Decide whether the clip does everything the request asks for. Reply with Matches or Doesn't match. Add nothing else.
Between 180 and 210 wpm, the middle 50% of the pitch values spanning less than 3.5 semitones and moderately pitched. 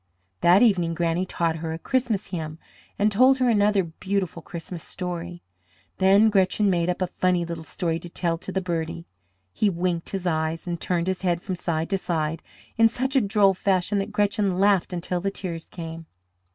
Matches